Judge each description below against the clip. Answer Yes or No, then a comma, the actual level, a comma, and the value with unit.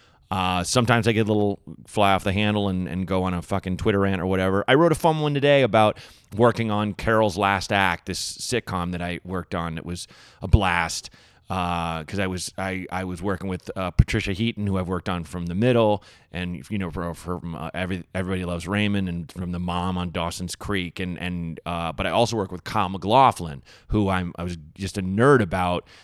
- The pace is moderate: No, fast, 220 wpm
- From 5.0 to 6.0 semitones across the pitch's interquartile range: No, average, 2.9 semitones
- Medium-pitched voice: No, very low, 95 Hz